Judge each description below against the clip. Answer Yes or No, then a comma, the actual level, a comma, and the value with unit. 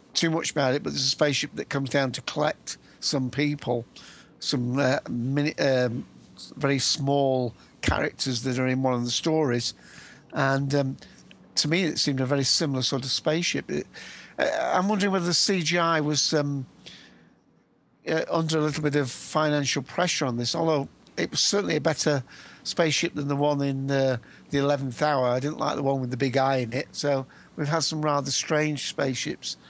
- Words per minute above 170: Yes, average, 190 wpm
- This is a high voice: No, medium, 140 Hz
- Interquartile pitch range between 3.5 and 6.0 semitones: No, average, 2.7 semitones